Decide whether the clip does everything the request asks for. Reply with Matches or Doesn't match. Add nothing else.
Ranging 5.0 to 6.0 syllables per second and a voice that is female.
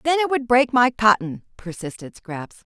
Doesn't match